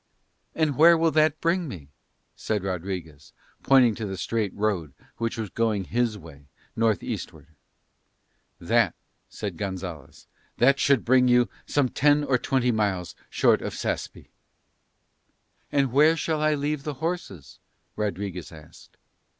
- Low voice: Yes, low, 115 Hz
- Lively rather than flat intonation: Yes, wide, 7.2 semitones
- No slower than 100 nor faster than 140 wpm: Yes, slow, 135 wpm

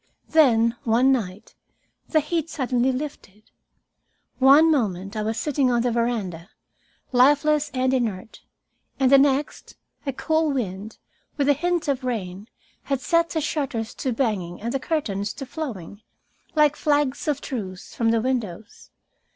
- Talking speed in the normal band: Yes, average, 145 wpm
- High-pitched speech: Yes, very high, 255 Hz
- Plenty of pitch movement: No, average, 4.8 semitones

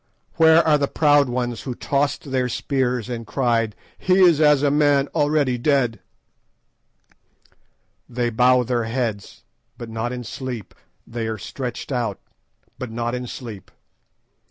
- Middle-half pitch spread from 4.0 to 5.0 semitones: No, average, 3.3 semitones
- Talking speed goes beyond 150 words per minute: No, average, 140 wpm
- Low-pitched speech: Yes, low, 125 Hz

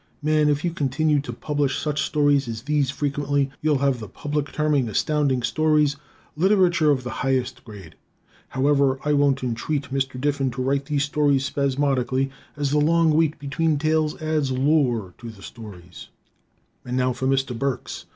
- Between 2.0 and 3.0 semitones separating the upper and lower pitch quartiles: Yes, narrow, 2.5 semitones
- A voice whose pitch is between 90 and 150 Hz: Yes, medium, 140 Hz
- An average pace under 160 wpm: No, average, 165 wpm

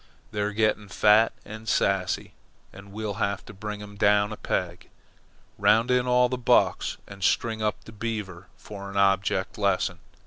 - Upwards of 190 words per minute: No, average, 165 wpm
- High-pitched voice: No, low, 105 Hz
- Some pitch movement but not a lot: No, narrow, 1.9 semitones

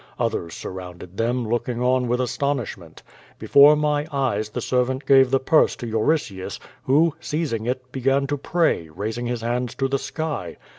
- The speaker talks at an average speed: Yes, average, 160 wpm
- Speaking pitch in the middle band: No, low, 125 Hz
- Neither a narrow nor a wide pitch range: Yes, average, 3.7 semitones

